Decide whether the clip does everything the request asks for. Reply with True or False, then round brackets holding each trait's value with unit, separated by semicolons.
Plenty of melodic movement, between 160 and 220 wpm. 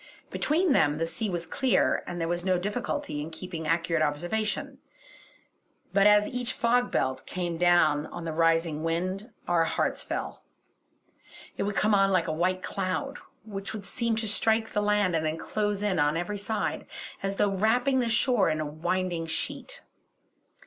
False (4.6 semitones; 175 wpm)